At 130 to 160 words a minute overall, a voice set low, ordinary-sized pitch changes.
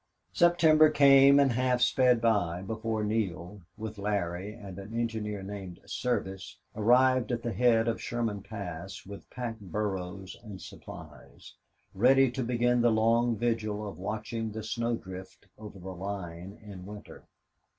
Yes: average, 145 wpm; low, 110 Hz; average, 3.4 semitones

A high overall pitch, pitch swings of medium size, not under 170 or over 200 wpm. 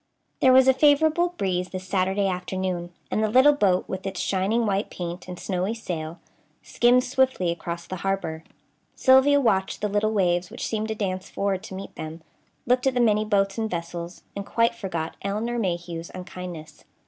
Yes: high, 195 Hz; average, 4.3 semitones; average, 180 wpm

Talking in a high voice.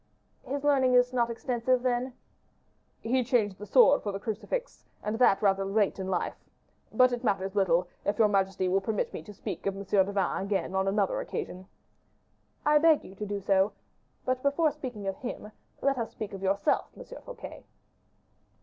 Yes: high, 210 Hz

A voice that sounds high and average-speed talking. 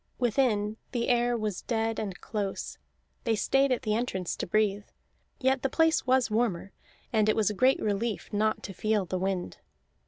Yes: high, 220 Hz; average, 180 wpm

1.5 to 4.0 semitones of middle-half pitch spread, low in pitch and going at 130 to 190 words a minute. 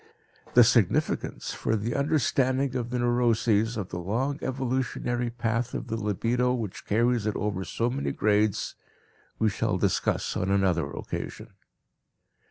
Yes: average, 3.0 semitones; low, 115 Hz; average, 140 wpm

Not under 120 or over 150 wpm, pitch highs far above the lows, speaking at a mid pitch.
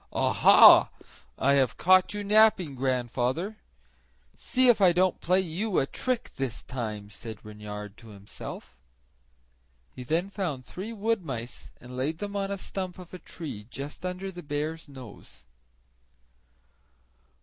Yes: average, 140 wpm; wide, 7.6 semitones; medium, 160 Hz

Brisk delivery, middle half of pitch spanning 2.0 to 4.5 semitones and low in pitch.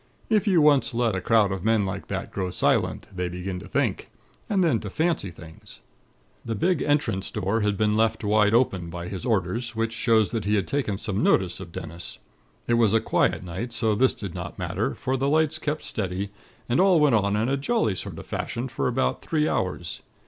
No: fast, 215 wpm; wide, 5.5 semitones; low, 110 Hz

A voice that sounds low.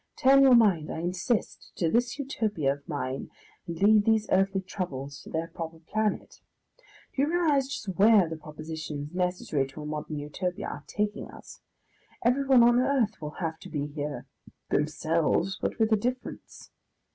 No: medium, 180 Hz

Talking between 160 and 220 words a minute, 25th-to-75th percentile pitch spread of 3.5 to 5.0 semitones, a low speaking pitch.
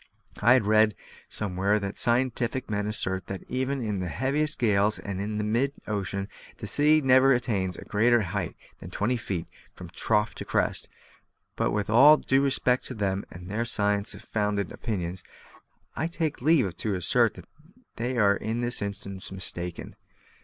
Yes: average, 165 wpm; average, 4.0 semitones; low, 105 Hz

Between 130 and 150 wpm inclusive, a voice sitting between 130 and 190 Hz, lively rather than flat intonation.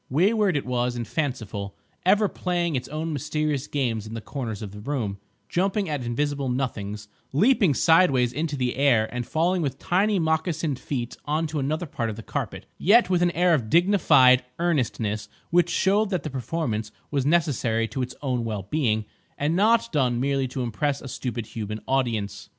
No: average, 180 wpm; medium, 140 Hz; wide, 5.8 semitones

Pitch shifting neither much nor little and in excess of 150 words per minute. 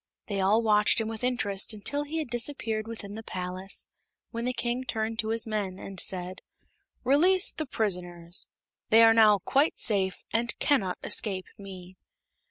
Yes: average, 3.7 semitones; average, 165 wpm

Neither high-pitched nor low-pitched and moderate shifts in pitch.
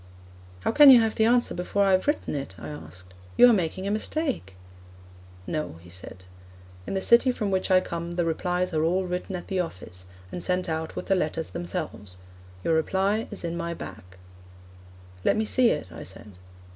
Yes: medium, 180 Hz; average, 4.8 semitones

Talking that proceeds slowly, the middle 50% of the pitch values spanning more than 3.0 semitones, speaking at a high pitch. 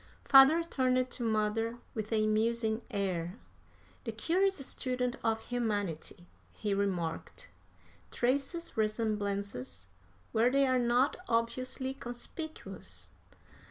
Yes: slow, 100 wpm; average, 3.4 semitones; high, 230 Hz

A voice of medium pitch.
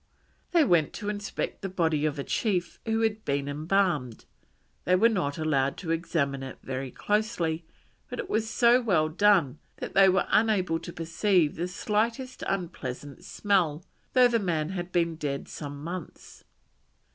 Yes: medium, 175 Hz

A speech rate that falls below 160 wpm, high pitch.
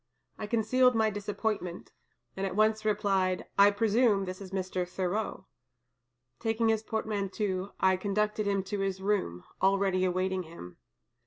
Yes: average, 140 wpm; high, 200 Hz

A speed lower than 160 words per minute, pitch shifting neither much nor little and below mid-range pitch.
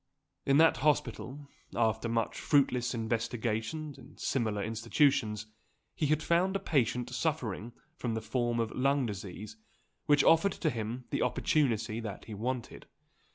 Yes: average, 140 wpm; average, 4.3 semitones; low, 120 Hz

